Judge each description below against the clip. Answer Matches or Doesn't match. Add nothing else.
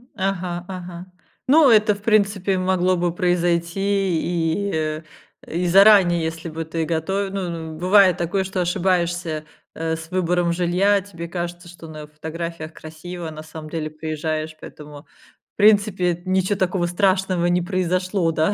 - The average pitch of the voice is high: Doesn't match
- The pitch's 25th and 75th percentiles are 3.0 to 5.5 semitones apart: Doesn't match